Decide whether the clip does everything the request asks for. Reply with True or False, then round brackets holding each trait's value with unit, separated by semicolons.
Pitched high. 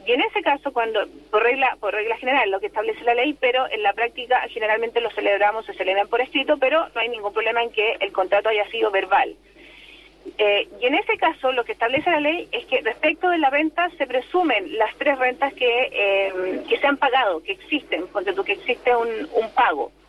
True (250 Hz)